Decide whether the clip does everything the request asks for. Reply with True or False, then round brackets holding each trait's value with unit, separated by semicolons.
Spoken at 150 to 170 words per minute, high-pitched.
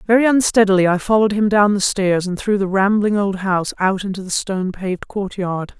False (205 wpm; 195 Hz)